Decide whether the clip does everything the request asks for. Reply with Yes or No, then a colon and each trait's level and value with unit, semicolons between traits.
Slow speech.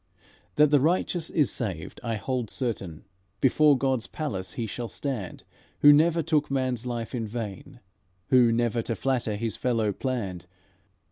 No: average, 150 wpm